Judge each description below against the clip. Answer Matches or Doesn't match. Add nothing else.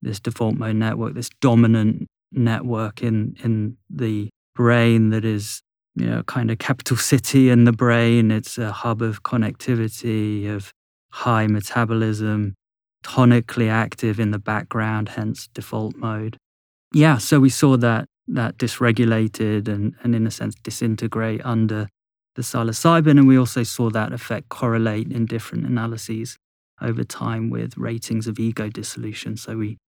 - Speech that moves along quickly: Doesn't match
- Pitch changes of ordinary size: Doesn't match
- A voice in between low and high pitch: Doesn't match